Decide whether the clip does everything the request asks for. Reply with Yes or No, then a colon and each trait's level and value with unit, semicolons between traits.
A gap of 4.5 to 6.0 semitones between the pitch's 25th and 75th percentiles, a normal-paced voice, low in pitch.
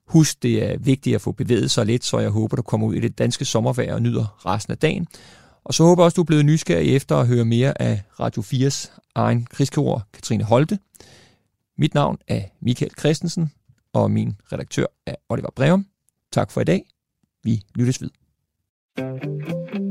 Yes: average, 5.2 semitones; average, 185 wpm; low, 130 Hz